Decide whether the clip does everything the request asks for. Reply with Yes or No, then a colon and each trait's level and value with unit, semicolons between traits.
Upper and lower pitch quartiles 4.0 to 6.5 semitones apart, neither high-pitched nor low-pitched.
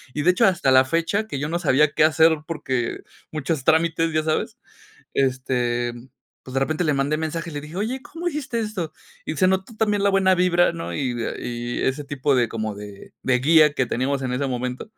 Yes: average, 5.1 semitones; medium, 150 Hz